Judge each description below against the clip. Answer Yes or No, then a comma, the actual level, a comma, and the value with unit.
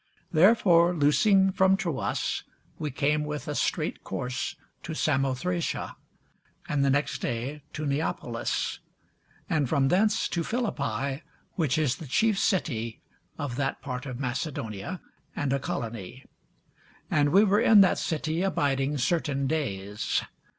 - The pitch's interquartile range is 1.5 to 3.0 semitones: No, average, 4.5 semitones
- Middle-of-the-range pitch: Yes, medium, 145 Hz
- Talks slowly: Yes, slow, 130 wpm